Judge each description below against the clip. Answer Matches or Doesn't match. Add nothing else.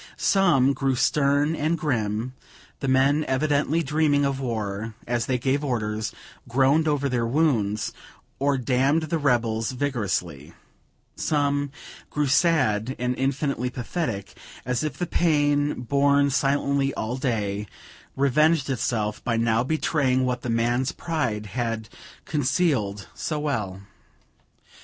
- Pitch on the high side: Doesn't match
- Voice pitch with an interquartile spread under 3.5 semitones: Doesn't match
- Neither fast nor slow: Doesn't match